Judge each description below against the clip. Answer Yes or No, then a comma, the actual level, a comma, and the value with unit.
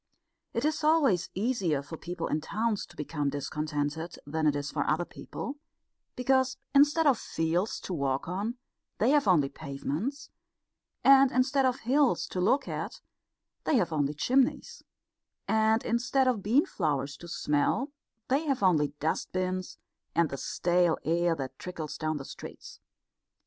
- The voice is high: No, medium, 180 Hz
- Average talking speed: Yes, average, 155 wpm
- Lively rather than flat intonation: Yes, wide, 8.8 semitones